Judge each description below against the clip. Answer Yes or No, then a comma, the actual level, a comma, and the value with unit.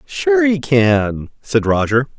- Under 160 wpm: Yes, slow, 135 wpm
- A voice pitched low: Yes, low, 130 Hz